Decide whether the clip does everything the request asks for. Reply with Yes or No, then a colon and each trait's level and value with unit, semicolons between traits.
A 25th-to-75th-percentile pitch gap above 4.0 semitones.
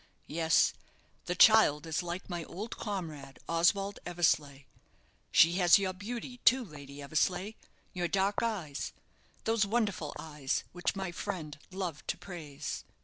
Yes: average, 4.4 semitones